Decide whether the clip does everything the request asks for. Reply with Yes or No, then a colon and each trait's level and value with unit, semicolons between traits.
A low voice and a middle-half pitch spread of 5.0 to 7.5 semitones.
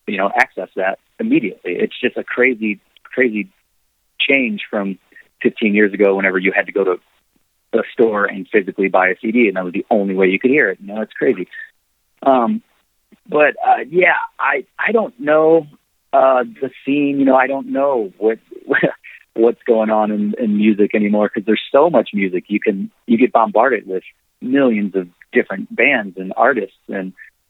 Yes: low, 110 Hz; wide, 5.6 semitones